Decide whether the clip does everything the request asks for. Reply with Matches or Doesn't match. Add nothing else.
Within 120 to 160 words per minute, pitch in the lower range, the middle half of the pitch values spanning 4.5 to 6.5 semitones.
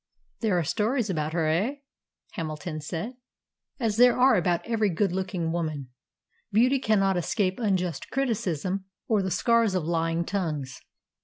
Doesn't match